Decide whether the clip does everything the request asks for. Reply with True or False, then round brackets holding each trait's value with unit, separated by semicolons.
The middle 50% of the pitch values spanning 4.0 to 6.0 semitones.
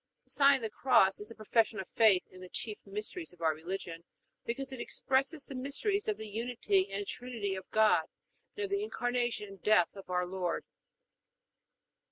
True (4.9 semitones)